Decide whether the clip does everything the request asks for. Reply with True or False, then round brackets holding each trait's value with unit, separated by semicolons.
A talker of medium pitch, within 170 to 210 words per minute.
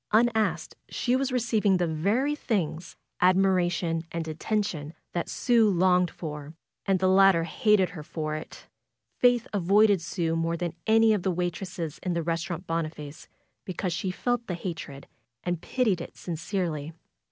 False (180 Hz; 155 wpm)